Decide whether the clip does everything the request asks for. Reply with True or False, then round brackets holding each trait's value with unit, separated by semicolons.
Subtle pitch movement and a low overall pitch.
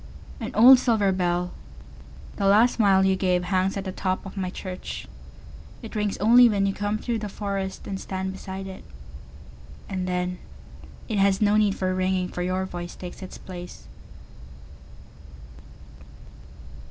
False (1.9 semitones; 190 Hz)